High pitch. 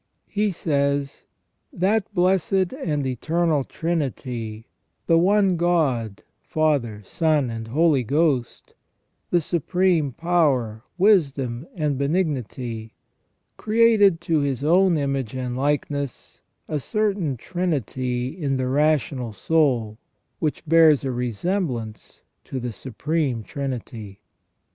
No: medium, 145 Hz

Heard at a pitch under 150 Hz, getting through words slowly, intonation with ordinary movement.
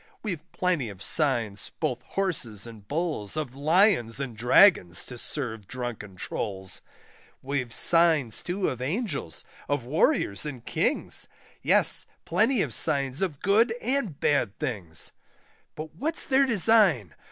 No: medium, 140 Hz; slow, 130 wpm; wide, 8.0 semitones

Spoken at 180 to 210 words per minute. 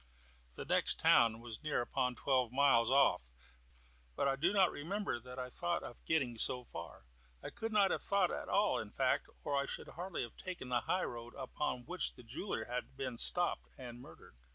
Yes: average, 200 wpm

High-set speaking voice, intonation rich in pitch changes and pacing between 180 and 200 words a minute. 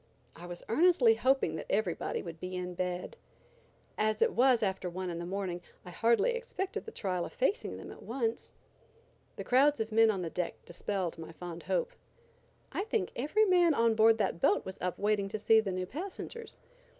Yes: high, 215 Hz; wide, 7.2 semitones; average, 195 wpm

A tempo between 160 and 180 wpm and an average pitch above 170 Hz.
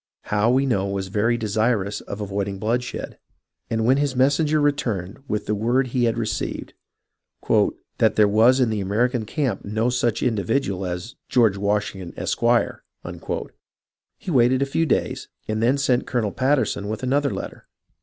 No: average, 165 wpm; low, 115 Hz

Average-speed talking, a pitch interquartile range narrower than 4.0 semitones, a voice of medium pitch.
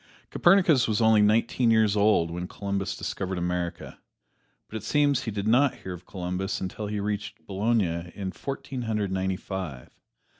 No: average, 160 wpm; average, 3.3 semitones; low, 100 Hz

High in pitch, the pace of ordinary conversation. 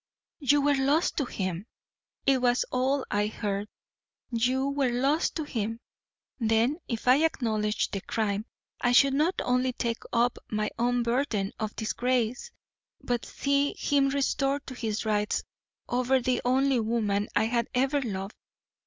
Yes: high, 245 Hz; average, 150 wpm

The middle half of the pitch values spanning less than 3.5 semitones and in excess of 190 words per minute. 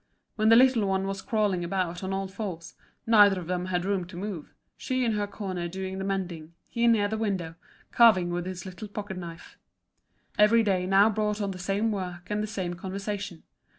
Yes: narrow, 2.6 semitones; average, 200 wpm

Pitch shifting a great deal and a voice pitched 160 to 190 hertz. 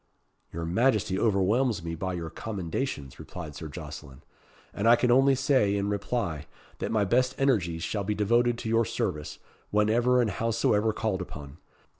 No: wide, 5.8 semitones; low, 105 Hz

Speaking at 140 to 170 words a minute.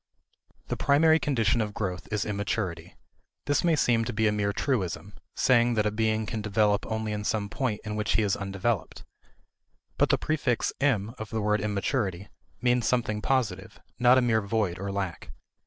No: average, 180 wpm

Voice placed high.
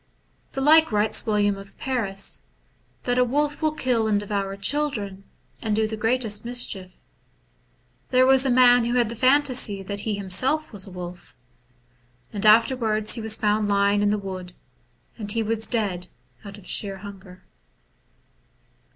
Yes: high, 215 Hz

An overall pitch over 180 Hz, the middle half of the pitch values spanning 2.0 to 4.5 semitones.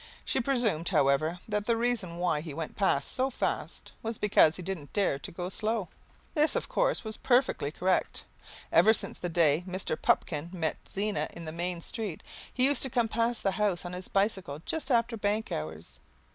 No: high, 190 Hz; wide, 5.4 semitones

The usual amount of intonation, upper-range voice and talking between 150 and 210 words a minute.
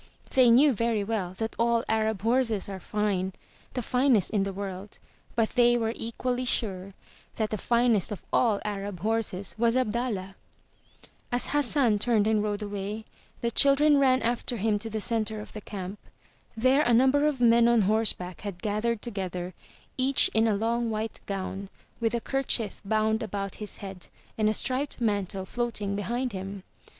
Yes: average, 3.0 semitones; high, 220 Hz; average, 170 wpm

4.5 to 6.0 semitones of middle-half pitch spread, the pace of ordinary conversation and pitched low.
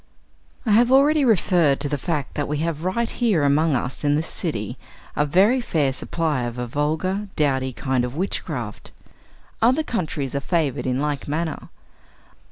No: average, 5.1 semitones; average, 170 wpm; medium, 150 Hz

